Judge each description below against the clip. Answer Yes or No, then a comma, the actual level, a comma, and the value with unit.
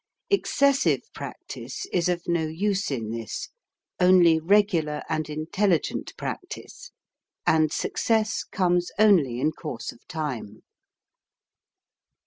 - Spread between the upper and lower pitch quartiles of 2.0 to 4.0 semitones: No, average, 4.4 semitones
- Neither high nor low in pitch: Yes, medium, 170 Hz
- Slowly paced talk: Yes, slow, 110 wpm